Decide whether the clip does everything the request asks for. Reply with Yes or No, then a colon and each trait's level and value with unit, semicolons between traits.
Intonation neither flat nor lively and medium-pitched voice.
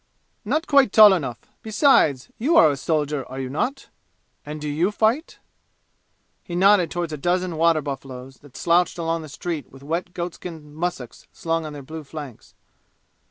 Yes: average, 3.7 semitones; medium, 160 Hz